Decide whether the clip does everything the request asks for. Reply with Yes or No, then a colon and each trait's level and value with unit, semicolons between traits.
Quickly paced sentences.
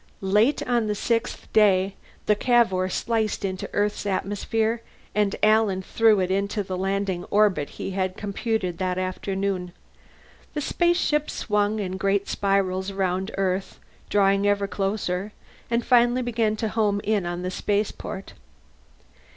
No: slow, 135 wpm